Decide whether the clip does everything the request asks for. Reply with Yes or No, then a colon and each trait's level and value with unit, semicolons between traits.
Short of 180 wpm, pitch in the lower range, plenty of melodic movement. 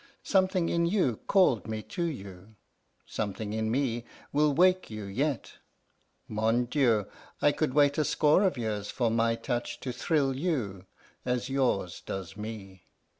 Yes: average, 150 wpm; low, 120 Hz; wide, 5.7 semitones